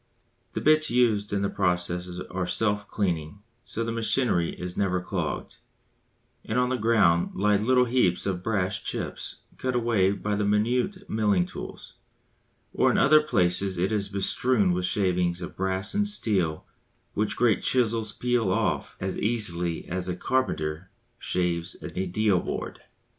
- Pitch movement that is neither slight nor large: Yes, average, 4.2 semitones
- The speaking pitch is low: Yes, low, 100 Hz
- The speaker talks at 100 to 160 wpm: Yes, average, 155 wpm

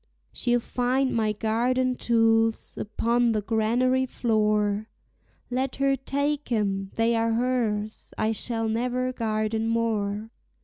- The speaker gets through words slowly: Yes, slow, 120 wpm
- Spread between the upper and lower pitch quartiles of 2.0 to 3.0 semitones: Yes, narrow, 2.6 semitones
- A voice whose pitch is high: Yes, high, 230 Hz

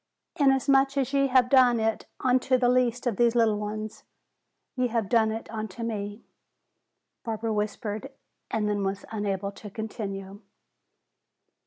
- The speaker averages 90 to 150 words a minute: Yes, average, 140 wpm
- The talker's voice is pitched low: No, high, 225 Hz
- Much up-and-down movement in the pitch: No, average, 3.3 semitones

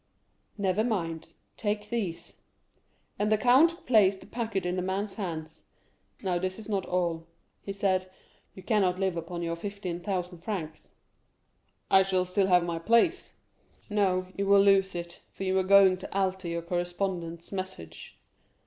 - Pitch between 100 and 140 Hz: No, high, 190 Hz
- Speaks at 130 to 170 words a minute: Yes, average, 155 wpm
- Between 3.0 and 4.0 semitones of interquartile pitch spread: No, narrow, 2.4 semitones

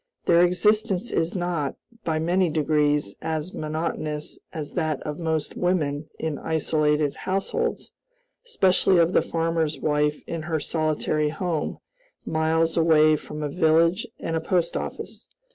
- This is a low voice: No, medium, 160 Hz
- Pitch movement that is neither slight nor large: No, narrow, 2.1 semitones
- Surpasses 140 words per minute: No, slow, 135 wpm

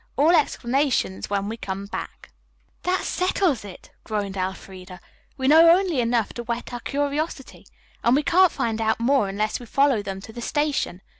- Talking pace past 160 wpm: Yes, average, 170 wpm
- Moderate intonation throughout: No, wide, 6.2 semitones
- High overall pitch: Yes, high, 240 Hz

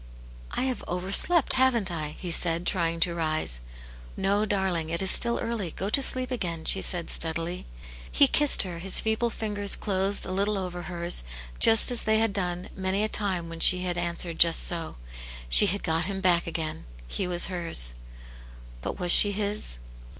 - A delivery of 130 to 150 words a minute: No, average, 190 wpm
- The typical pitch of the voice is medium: Yes, medium, 180 Hz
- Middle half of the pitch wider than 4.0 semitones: No, average, 3.4 semitones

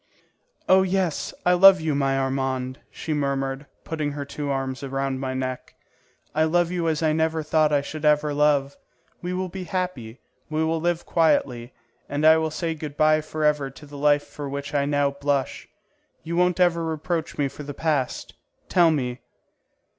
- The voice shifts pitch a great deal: No, average, 2.7 semitones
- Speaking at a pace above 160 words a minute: Yes, average, 180 wpm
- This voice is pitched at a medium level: Yes, medium, 150 Hz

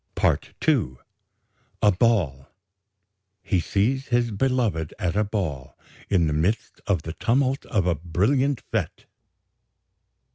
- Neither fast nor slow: No, slow, 120 wpm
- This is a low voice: Yes, low, 100 Hz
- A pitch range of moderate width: No, wide, 6.5 semitones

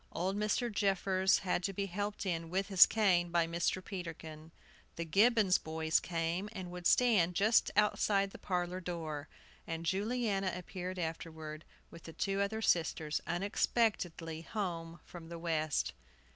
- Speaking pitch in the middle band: Yes, medium, 180 Hz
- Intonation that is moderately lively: Yes, average, 3.2 semitones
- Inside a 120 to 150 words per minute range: Yes, average, 145 wpm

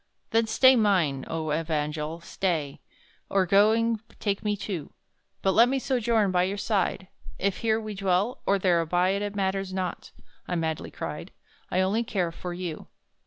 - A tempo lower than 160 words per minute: No, average, 165 wpm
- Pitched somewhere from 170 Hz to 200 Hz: Yes, high, 190 Hz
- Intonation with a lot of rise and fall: No, average, 3.5 semitones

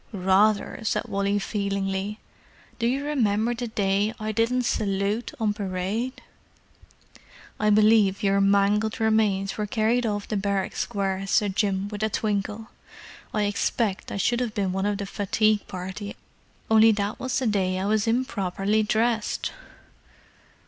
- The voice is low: No, high, 210 Hz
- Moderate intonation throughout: No, narrow, 1.9 semitones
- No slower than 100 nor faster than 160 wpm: Yes, average, 145 wpm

